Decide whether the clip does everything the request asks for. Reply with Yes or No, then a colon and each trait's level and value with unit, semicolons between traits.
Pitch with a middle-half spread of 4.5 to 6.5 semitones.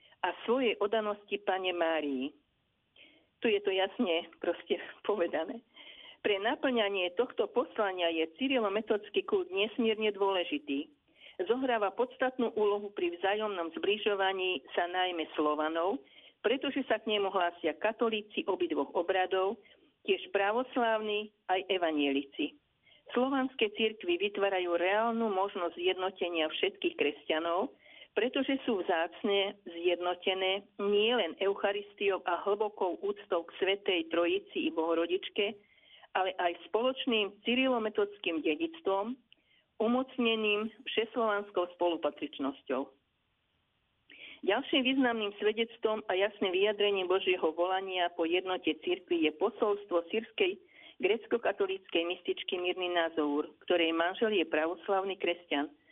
Yes: average, 5.2 semitones